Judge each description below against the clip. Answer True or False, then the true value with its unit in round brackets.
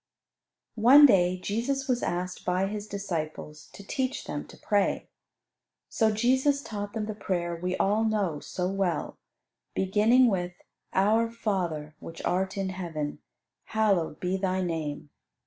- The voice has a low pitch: False (195 Hz)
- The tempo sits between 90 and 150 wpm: True (140 wpm)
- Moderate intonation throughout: True (3.6 semitones)